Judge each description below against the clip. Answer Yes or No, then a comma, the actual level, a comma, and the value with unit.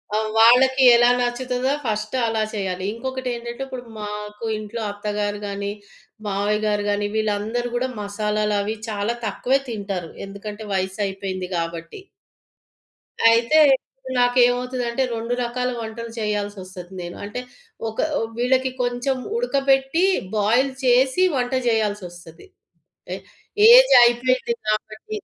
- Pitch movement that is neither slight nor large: Yes, average, 3.4 semitones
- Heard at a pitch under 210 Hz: No, high, 225 Hz